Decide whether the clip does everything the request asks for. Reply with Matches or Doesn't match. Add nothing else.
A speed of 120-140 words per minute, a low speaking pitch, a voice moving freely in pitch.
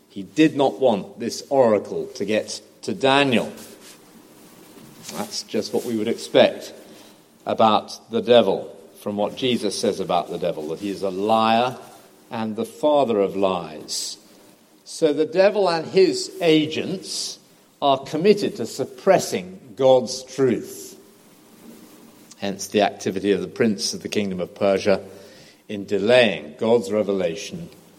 Matches